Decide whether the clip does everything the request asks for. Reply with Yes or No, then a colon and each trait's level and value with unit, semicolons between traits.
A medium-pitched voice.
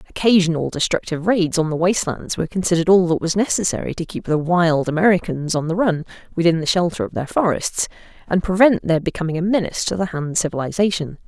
Yes: medium, 175 Hz